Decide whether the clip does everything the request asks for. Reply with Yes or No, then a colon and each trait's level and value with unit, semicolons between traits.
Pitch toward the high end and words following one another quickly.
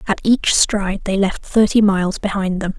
No: high, 200 Hz; average, 195 wpm